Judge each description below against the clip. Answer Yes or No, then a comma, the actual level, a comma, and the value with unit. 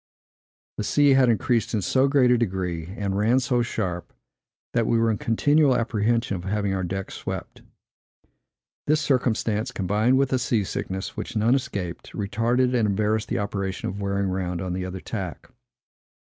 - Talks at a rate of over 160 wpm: Yes, average, 170 wpm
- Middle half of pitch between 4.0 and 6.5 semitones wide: Yes, average, 4.3 semitones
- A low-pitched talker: Yes, low, 110 Hz